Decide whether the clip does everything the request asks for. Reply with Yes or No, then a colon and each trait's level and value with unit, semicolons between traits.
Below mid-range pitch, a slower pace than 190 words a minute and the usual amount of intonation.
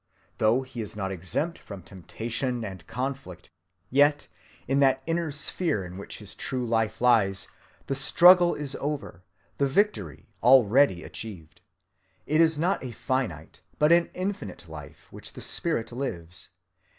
No: low, 125 Hz; average, 145 wpm; wide, 6.6 semitones